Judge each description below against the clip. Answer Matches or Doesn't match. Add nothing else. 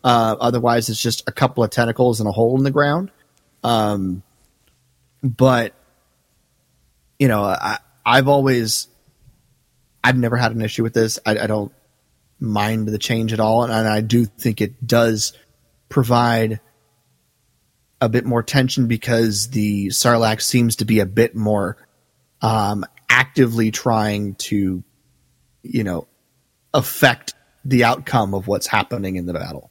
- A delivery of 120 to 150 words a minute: Matches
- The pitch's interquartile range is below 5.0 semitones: Matches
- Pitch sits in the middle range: Doesn't match